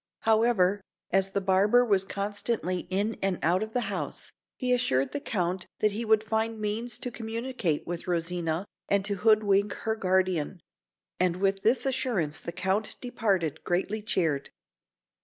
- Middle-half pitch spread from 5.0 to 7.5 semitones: No, average, 3.3 semitones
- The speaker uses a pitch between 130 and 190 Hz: No, high, 200 Hz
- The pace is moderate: Yes, average, 160 wpm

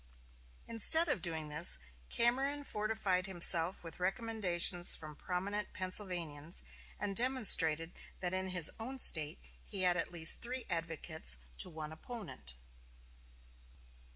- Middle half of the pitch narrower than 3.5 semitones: No, average, 5.0 semitones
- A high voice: No, medium, 180 Hz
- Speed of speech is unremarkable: No, slow, 120 wpm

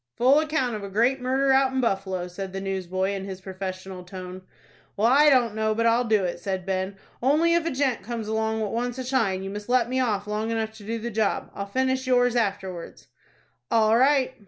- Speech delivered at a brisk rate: Yes, fast, 220 wpm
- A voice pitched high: Yes, high, 220 Hz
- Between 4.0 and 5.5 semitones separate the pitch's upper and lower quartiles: Yes, average, 4.7 semitones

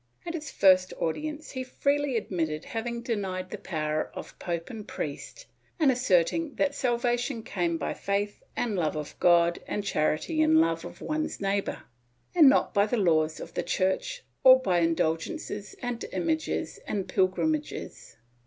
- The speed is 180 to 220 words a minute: No, average, 155 wpm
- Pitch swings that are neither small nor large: No, wide, 7.9 semitones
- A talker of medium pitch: No, high, 205 Hz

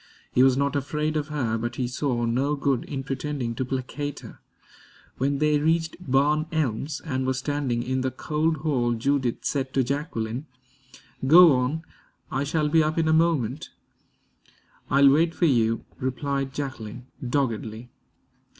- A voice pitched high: No, medium, 140 Hz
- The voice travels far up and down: No, average, 3.2 semitones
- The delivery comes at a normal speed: Yes, average, 155 wpm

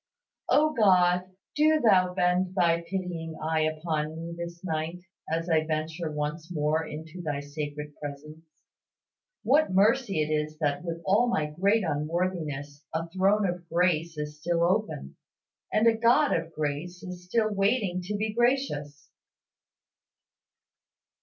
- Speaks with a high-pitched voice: No, medium, 170 Hz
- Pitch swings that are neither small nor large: Yes, average, 3.6 semitones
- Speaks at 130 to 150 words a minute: Yes, average, 140 wpm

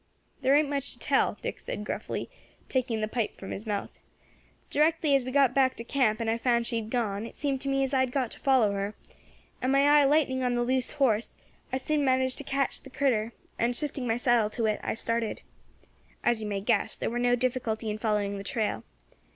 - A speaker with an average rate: No, fast, 225 wpm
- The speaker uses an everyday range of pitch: Yes, average, 3.6 semitones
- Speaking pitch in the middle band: No, high, 245 Hz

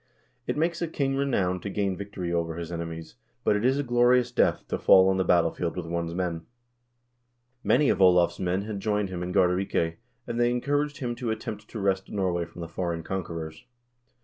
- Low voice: Yes, very low, 95 Hz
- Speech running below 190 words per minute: No, average, 200 wpm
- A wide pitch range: Yes, wide, 5.7 semitones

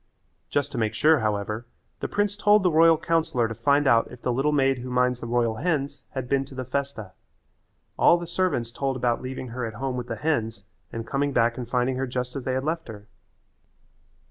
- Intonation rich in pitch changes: No, average, 3.5 semitones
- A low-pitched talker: Yes, low, 130 Hz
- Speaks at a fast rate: Yes, fast, 220 wpm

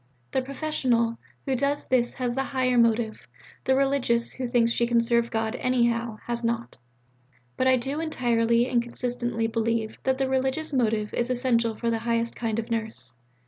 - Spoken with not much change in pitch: Yes, narrow, 2.0 semitones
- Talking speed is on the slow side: No, average, 175 wpm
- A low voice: No, high, 235 Hz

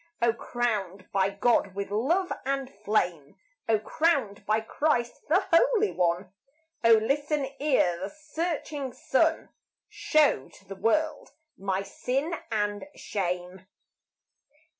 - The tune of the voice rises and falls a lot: Yes, wide, 7.1 semitones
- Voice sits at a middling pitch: No, high, 225 Hz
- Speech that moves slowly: Yes, slow, 120 wpm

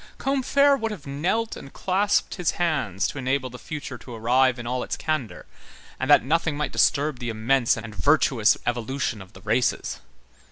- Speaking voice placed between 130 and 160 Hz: Yes, low, 135 Hz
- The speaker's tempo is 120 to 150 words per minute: No, average, 175 wpm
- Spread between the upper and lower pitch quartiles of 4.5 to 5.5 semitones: Yes, average, 5.1 semitones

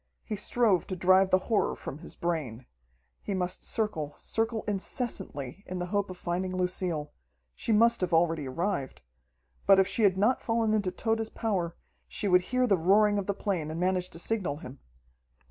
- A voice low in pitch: No, medium, 185 Hz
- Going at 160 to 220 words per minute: Yes, average, 180 wpm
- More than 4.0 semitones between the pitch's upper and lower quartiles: No, average, 3.5 semitones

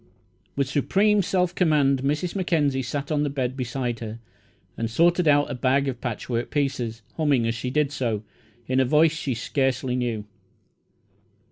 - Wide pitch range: No, average, 3.5 semitones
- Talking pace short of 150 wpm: No, average, 160 wpm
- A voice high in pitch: No, low, 135 Hz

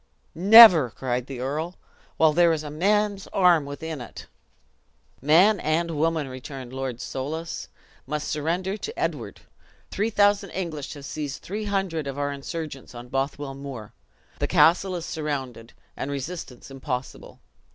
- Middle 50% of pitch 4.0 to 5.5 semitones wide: Yes, average, 4.6 semitones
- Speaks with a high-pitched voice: No, medium, 150 Hz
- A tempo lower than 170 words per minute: Yes, average, 140 wpm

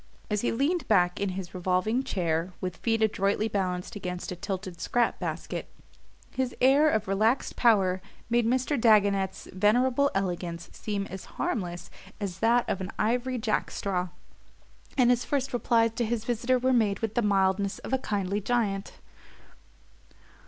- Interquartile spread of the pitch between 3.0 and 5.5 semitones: Yes, average, 4.2 semitones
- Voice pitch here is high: Yes, high, 210 Hz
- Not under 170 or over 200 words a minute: No, average, 155 wpm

